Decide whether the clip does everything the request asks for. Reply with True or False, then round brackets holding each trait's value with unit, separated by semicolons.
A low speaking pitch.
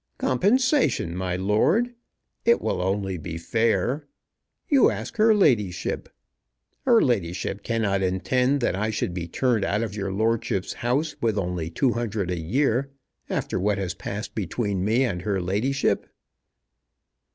True (105 Hz)